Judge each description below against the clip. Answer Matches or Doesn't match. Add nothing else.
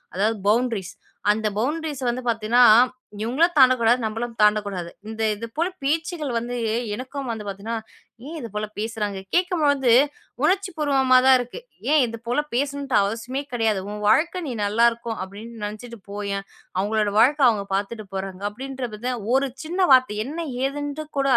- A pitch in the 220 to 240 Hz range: Matches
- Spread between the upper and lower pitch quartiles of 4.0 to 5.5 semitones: Matches